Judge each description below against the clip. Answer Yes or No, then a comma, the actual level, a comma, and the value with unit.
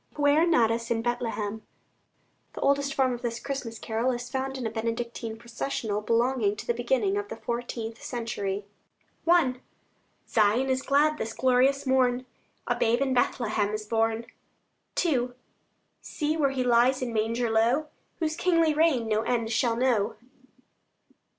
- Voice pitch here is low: No, high, 240 Hz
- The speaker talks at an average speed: Yes, average, 150 wpm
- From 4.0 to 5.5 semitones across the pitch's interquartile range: No, average, 2.8 semitones